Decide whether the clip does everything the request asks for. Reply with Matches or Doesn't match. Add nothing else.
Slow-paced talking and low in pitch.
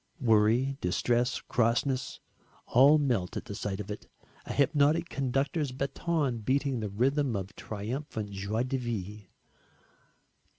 Matches